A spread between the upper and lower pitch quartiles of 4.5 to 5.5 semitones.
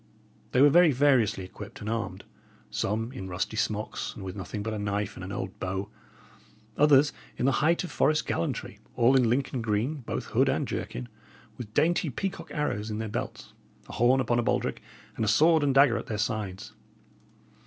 Yes: average, 5.0 semitones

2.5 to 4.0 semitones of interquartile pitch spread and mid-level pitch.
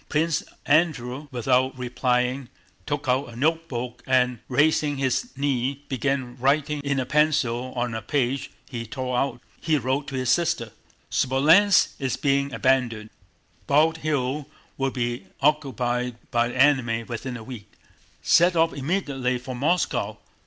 No: average, 2.9 semitones; low, 130 Hz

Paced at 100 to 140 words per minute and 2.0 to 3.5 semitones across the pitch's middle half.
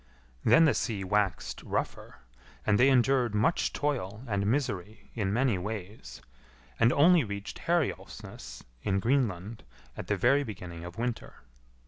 No: slow, 135 wpm; average, 5.3 semitones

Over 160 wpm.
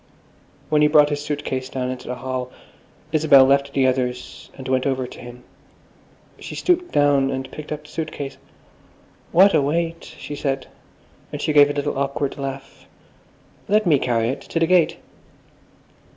Yes: average, 175 wpm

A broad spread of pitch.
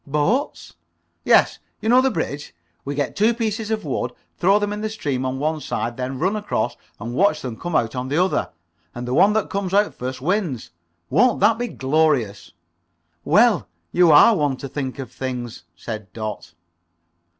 Yes: wide, 8.4 semitones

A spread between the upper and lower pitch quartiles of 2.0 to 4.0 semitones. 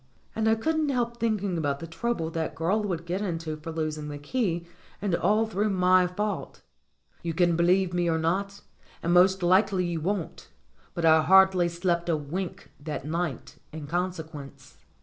Yes: average, 3.3 semitones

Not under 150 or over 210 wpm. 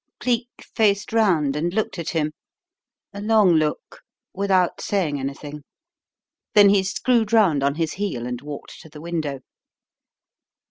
No: average, 140 wpm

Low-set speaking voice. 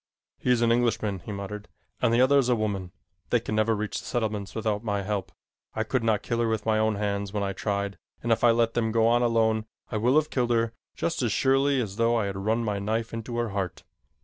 Yes: low, 110 Hz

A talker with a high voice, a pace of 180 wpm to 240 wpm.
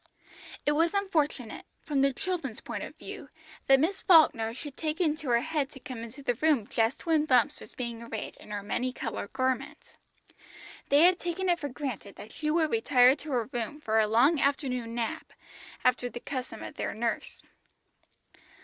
Yes: very high, 270 Hz; average, 185 wpm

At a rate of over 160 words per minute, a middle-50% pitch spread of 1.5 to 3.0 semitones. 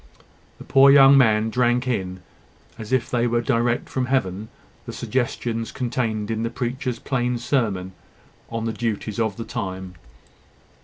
No: average, 150 wpm; narrow, 2.5 semitones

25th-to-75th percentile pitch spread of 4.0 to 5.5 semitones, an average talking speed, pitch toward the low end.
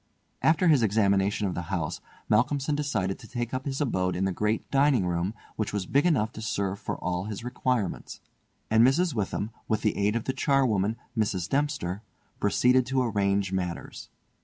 Yes: average, 5.1 semitones; average, 180 wpm; low, 110 Hz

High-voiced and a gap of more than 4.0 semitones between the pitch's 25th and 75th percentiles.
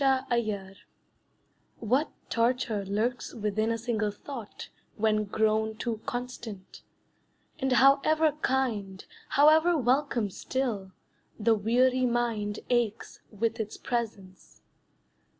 No: high, 230 Hz; average, 3.3 semitones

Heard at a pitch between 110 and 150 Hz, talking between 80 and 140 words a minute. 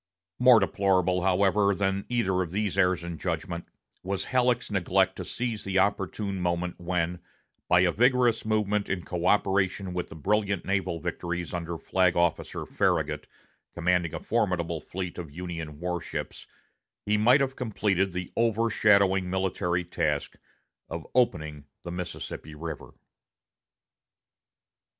No: very low, 95 Hz; slow, 135 wpm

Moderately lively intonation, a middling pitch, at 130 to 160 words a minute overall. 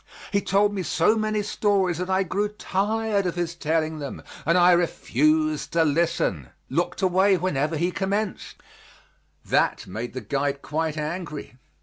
Yes: average, 4.1 semitones; medium, 175 Hz; average, 150 wpm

